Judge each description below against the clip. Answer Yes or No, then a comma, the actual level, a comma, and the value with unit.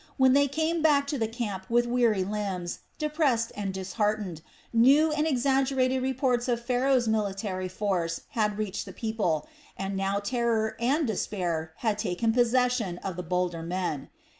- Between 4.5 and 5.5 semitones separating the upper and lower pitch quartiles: Yes, average, 5.1 semitones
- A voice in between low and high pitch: No, high, 220 Hz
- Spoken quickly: No, average, 155 wpm